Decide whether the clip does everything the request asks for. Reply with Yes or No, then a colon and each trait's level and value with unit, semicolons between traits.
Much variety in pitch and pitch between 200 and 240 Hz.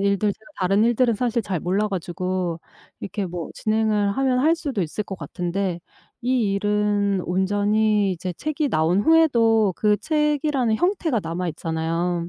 No: average, 4.4 semitones; high, 205 Hz